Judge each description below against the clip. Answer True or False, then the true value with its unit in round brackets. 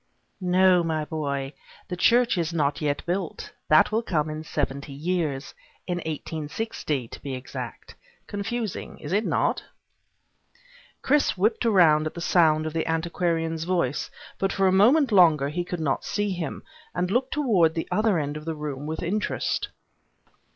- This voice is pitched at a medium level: True (165 Hz)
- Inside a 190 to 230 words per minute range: False (165 wpm)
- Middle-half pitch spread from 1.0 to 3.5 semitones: False (4.0 semitones)